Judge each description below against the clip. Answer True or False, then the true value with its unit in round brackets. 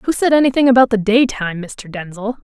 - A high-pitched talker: True (230 Hz)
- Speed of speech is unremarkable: True (195 wpm)